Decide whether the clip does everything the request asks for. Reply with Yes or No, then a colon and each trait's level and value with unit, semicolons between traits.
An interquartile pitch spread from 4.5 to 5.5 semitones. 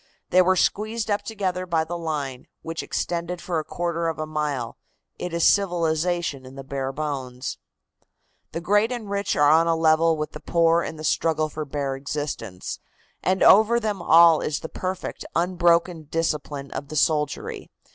No: average, 3.1 semitones